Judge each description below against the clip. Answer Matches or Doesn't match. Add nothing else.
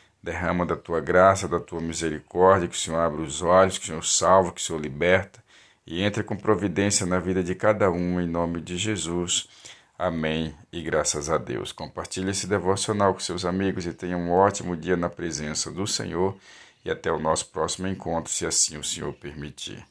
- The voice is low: Matches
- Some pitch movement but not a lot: Doesn't match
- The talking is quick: Matches